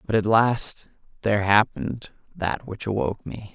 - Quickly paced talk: No, average, 150 wpm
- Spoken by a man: Yes, male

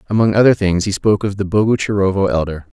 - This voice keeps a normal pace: Yes, average, 195 wpm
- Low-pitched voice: Yes, low, 100 Hz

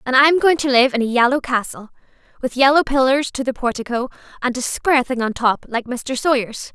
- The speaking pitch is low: No, very high, 255 Hz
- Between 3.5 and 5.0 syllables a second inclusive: No, 5.6 syllables/s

